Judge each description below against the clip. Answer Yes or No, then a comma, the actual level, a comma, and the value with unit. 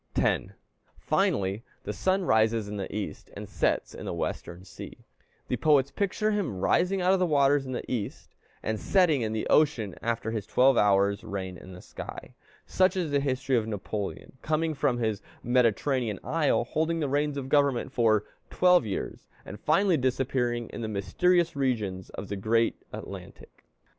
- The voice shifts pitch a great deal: Yes, wide, 6.1 semitones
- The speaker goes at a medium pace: Yes, average, 175 wpm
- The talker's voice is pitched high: No, low, 125 Hz